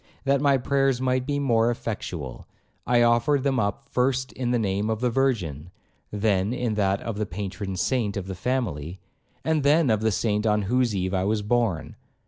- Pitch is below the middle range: Yes, low, 115 Hz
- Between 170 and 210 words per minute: Yes, average, 190 wpm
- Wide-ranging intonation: No, average, 4.4 semitones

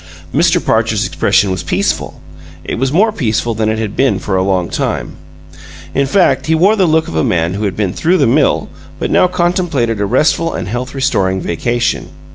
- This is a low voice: Yes, low, 120 Hz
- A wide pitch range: Yes, wide, 8.0 semitones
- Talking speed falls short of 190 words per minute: No, average, 200 wpm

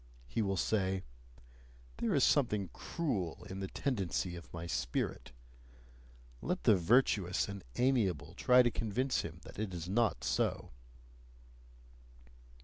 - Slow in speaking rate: Yes, slow, 130 wpm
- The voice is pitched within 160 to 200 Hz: No, very low, 95 Hz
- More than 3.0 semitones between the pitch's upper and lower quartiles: Yes, average, 5.1 semitones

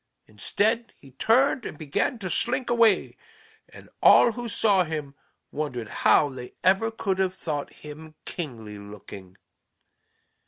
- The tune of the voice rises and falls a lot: Yes, wide, 8.9 semitones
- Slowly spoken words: Yes, slow, 130 wpm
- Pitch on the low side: No, medium, 160 Hz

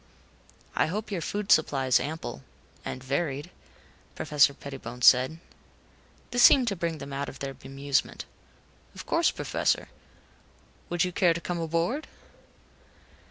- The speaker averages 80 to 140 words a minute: Yes, slow, 135 wpm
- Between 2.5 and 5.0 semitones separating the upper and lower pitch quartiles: Yes, average, 4.2 semitones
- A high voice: No, medium, 155 Hz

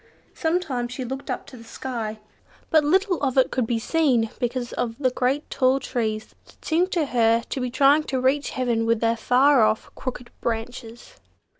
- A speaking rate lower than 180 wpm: No, average, 185 wpm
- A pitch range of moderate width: Yes, average, 3.4 semitones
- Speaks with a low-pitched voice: No, very high, 255 Hz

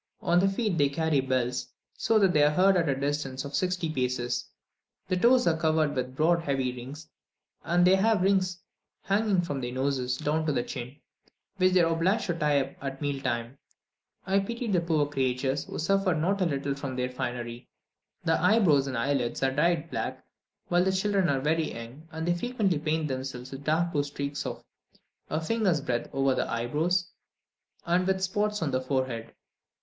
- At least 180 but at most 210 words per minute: Yes, average, 190 wpm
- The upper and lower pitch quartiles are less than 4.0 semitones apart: No, average, 5.3 semitones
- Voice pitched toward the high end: No, medium, 155 Hz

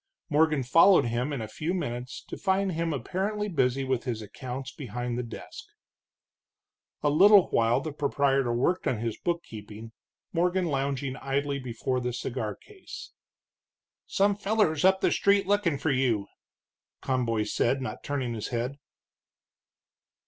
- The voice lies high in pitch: No, low, 135 Hz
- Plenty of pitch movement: Yes, wide, 5.9 semitones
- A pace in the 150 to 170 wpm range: No, average, 140 wpm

